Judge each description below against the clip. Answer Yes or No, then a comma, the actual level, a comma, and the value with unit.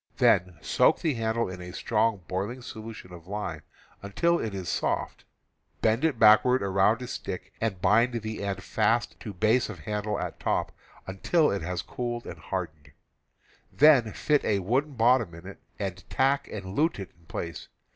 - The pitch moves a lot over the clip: No, average, 4.2 semitones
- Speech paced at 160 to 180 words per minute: Yes, average, 175 wpm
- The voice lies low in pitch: Yes, low, 105 Hz